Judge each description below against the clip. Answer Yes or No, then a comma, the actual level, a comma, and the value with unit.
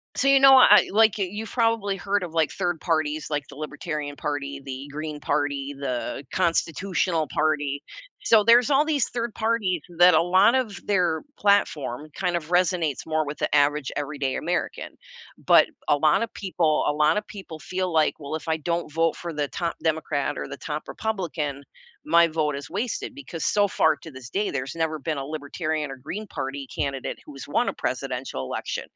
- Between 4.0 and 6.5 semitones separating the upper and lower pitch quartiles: Yes, average, 4.7 semitones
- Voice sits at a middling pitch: Yes, medium, 160 Hz